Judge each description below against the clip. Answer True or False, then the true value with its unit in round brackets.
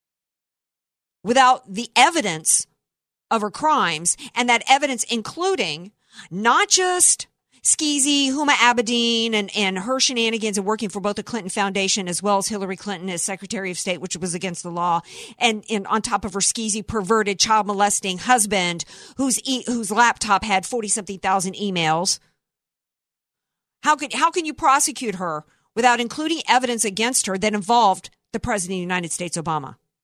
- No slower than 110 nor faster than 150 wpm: False (160 wpm)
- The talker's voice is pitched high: True (215 Hz)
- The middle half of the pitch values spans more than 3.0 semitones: True (4.1 semitones)